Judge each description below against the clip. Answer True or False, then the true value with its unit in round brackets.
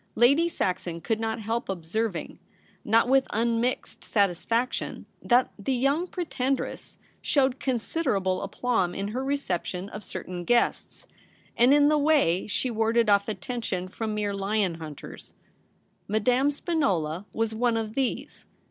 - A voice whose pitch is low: False (225 Hz)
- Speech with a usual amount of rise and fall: True (4.7 semitones)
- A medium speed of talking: False (130 wpm)